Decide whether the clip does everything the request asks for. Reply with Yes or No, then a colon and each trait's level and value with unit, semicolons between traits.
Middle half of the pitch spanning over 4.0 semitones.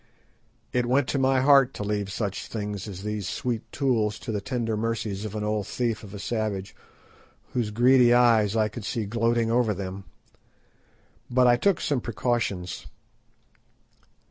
No: average, 2.9 semitones